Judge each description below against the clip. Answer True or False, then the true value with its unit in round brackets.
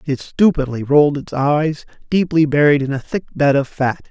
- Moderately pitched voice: True (145 Hz)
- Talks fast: False (190 wpm)